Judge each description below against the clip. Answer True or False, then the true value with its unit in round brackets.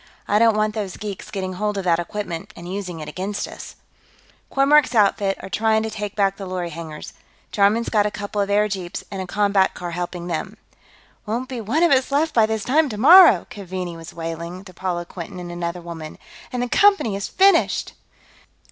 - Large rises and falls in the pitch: False (3.7 semitones)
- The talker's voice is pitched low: False (200 Hz)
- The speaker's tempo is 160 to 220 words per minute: True (200 wpm)